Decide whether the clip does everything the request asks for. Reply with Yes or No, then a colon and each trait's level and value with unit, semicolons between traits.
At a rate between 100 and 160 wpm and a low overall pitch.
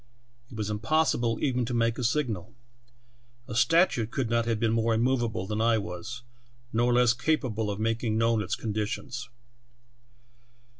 Yes: average, 150 wpm; low, 115 Hz